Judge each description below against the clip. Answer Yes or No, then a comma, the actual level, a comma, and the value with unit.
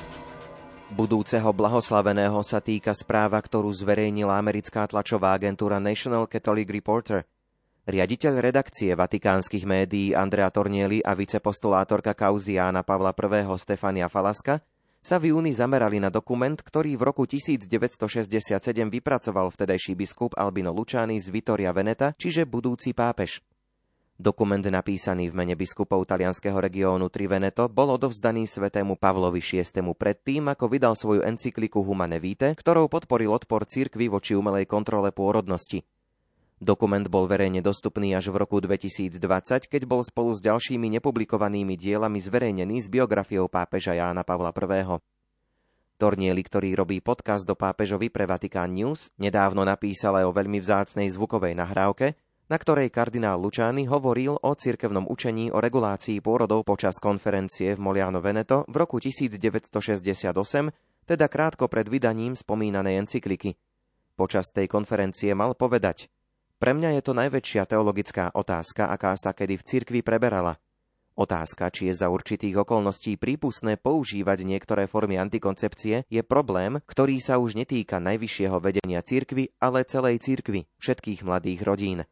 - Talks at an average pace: Yes, average, 135 wpm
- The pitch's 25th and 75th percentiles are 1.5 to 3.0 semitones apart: No, average, 3.6 semitones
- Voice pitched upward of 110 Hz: No, low, 105 Hz